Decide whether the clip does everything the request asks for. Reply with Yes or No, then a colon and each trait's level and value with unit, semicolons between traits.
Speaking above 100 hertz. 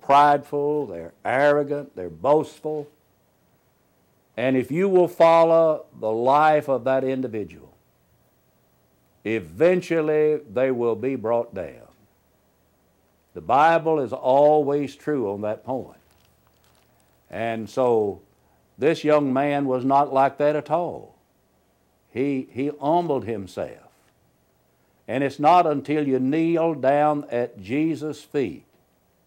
Yes: medium, 140 Hz